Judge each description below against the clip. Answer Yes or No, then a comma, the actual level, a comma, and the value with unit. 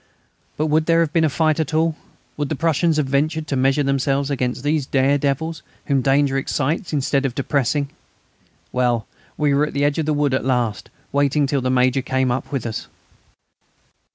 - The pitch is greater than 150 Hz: No, medium, 140 Hz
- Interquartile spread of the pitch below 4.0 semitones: Yes, narrow, 2.5 semitones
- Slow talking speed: No, average, 195 wpm